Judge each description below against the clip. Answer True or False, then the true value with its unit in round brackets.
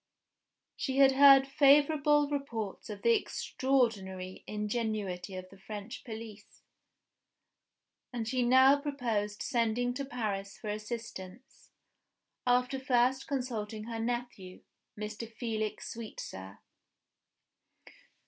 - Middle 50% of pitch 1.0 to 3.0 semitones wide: False (3.9 semitones)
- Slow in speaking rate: True (100 wpm)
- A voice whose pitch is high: True (230 Hz)